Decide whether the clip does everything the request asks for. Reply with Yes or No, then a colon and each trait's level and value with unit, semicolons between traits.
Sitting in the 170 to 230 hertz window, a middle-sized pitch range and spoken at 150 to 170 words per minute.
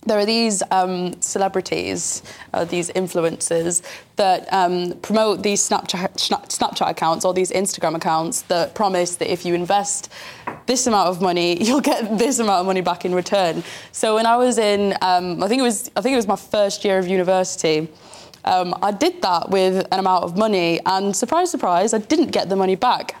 No: high, 190 Hz; average, 3.3 semitones; average, 195 wpm